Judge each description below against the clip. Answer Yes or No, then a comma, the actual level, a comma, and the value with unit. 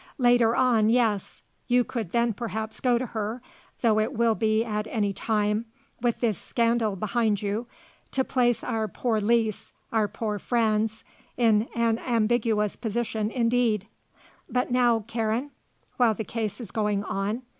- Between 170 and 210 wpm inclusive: No, average, 150 wpm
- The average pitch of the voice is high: Yes, high, 225 Hz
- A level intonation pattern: Yes, narrow, 2.0 semitones